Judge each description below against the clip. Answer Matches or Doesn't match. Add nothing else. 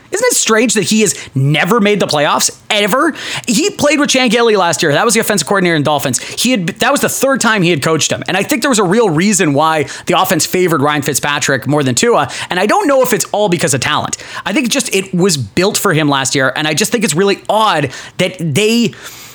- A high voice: Matches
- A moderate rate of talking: Doesn't match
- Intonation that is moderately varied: Doesn't match